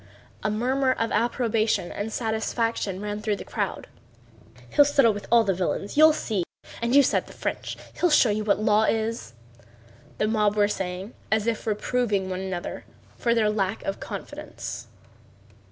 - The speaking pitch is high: Yes, high, 215 Hz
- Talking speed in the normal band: Yes, average, 165 wpm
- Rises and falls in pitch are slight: Yes, narrow, 2.3 semitones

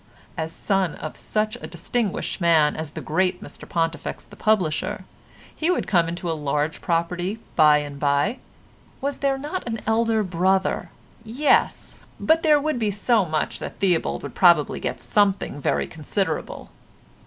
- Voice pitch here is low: No, medium, 185 Hz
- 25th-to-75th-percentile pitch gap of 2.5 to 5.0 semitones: No, wide, 5.5 semitones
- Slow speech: No, average, 155 wpm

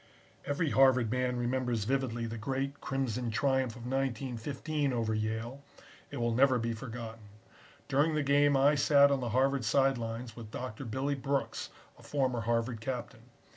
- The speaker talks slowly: No, average, 160 wpm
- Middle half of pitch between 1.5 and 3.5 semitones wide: Yes, average, 2.9 semitones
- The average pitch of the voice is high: No, low, 125 Hz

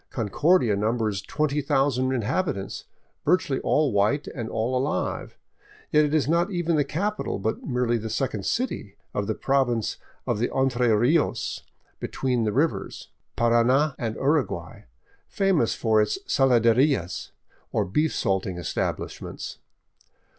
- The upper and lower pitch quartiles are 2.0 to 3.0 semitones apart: No, average, 5.1 semitones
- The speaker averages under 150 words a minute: Yes, average, 140 wpm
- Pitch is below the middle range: Yes, low, 125 Hz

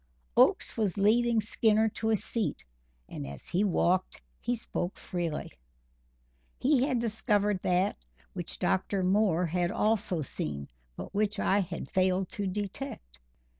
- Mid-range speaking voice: No, high, 200 Hz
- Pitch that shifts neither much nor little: Yes, average, 3.5 semitones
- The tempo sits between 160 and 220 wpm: No, slow, 135 wpm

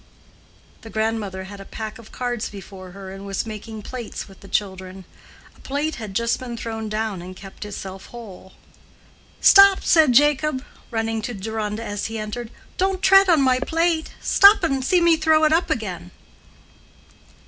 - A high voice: Yes, high, 225 Hz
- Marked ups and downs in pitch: Yes, wide, 6.5 semitones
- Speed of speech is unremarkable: Yes, average, 170 wpm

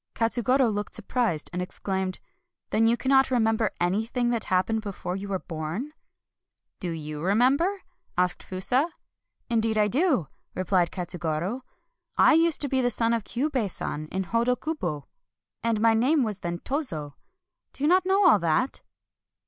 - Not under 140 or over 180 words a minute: Yes, average, 175 wpm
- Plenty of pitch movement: Yes, wide, 6.1 semitones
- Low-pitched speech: No, high, 225 Hz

